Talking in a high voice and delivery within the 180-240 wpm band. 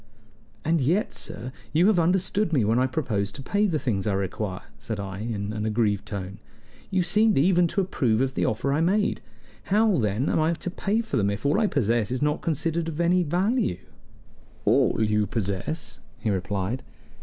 No: low, 135 Hz; average, 200 wpm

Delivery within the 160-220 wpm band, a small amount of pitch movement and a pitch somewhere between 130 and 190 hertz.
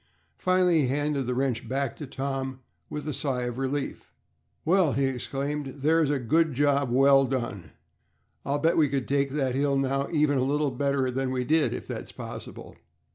Yes: average, 185 wpm; narrow, 2.0 semitones; medium, 140 Hz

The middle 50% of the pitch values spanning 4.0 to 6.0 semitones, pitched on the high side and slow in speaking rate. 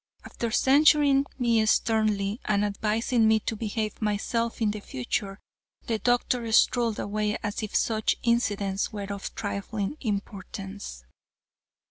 No: narrow, 2.4 semitones; high, 215 Hz; slow, 125 wpm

